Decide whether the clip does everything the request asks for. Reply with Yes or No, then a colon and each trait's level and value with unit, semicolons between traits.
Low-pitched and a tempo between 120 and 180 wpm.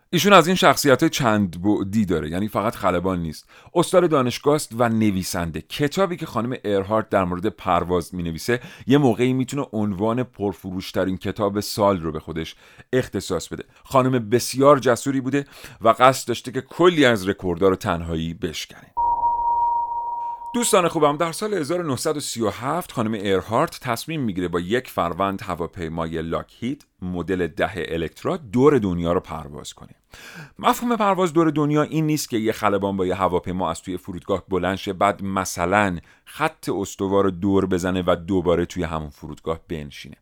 Yes: low, 105 Hz; average, 150 wpm